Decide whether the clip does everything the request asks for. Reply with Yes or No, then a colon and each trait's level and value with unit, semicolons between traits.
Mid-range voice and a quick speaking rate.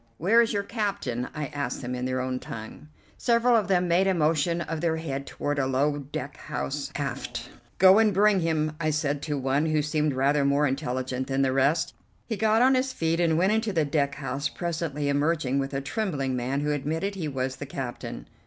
Yes: medium, 150 Hz; fast, 210 wpm